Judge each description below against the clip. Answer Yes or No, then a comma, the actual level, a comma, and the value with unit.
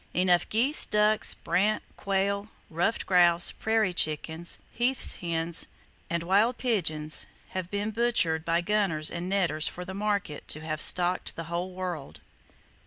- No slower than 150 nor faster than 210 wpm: No, average, 140 wpm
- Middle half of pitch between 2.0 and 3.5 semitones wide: No, average, 3.9 semitones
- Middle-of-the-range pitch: Yes, medium, 180 Hz